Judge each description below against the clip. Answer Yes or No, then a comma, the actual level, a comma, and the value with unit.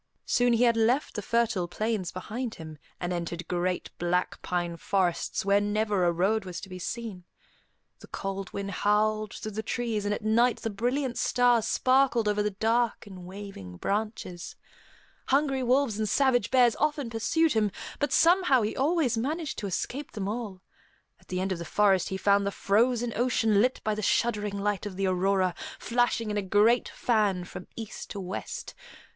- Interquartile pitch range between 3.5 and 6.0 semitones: Yes, average, 3.9 semitones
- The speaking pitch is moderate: No, high, 210 Hz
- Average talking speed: Yes, average, 180 wpm